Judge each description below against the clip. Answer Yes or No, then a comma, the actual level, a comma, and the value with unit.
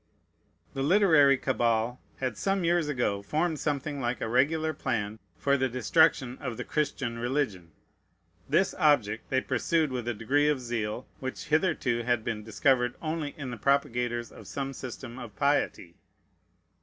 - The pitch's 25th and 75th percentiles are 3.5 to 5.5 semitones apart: Yes, average, 3.8 semitones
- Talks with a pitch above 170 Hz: No, low, 130 Hz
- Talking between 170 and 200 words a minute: No, average, 155 wpm